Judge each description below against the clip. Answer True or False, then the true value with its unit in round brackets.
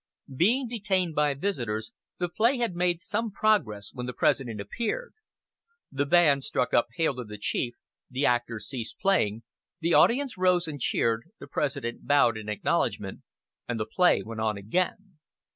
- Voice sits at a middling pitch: True (145 Hz)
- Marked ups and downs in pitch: True (8.2 semitones)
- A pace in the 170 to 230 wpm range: False (160 wpm)